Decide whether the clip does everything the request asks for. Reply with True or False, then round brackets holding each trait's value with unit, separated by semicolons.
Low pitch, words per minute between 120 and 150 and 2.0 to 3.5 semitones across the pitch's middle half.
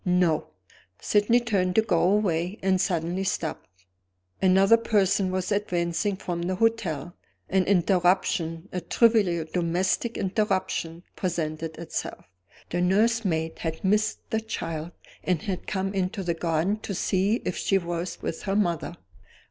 False (185 Hz; 135 wpm; 3.0 semitones)